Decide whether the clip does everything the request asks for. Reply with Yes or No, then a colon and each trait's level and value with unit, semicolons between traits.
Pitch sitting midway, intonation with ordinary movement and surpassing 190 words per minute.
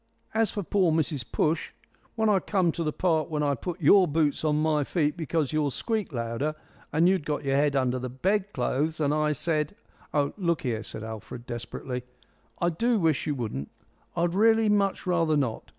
Yes: medium, 155 Hz; average, 4.2 semitones; average, 200 wpm